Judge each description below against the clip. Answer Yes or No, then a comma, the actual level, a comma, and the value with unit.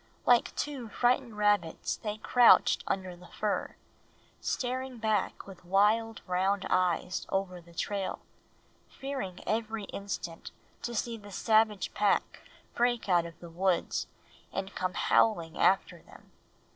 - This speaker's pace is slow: Yes, slow, 130 wpm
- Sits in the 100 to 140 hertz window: No, high, 205 Hz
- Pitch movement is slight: No, average, 3.6 semitones